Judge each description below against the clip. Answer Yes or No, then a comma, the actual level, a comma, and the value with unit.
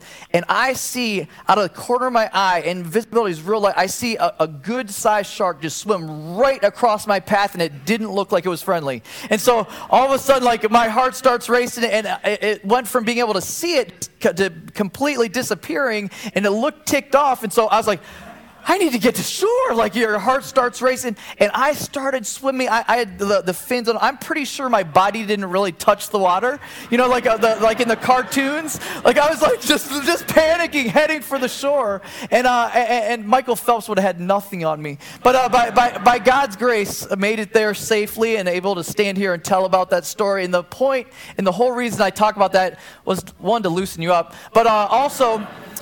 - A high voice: Yes, high, 225 Hz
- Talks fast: Yes, fast, 230 wpm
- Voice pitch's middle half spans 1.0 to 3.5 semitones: No, average, 4.4 semitones